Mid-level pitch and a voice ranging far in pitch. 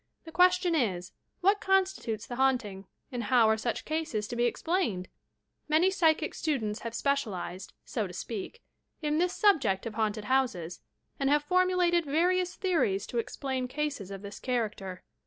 No: very high, 260 Hz; wide, 7.9 semitones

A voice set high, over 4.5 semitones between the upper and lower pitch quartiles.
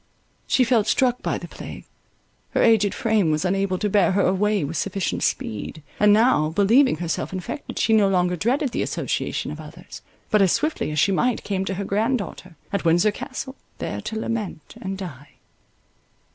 No: high, 200 Hz; average, 3.7 semitones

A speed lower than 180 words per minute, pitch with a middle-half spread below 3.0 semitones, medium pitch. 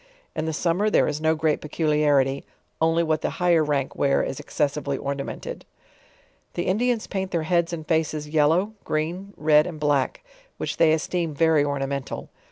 Yes: average, 165 wpm; narrow, 2.5 semitones; medium, 155 Hz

